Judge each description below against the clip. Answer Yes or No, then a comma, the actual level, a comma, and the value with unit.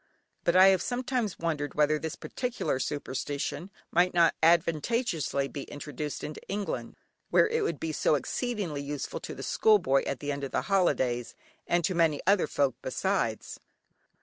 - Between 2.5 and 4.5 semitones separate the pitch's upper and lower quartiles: No, average, 5.2 semitones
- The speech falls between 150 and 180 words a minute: Yes, average, 165 wpm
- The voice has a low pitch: No, medium, 160 Hz